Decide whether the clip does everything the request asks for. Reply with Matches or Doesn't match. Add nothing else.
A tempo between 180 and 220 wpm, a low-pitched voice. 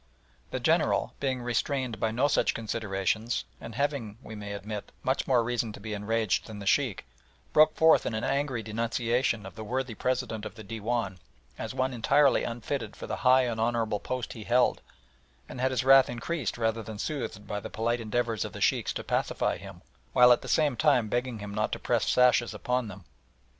Matches